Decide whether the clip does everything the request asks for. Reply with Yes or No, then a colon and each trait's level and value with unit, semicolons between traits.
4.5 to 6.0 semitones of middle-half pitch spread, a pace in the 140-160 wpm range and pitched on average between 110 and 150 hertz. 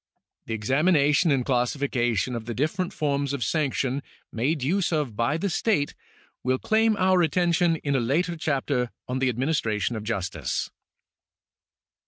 Yes: average, 5.1 semitones; average, 145 wpm; medium, 140 Hz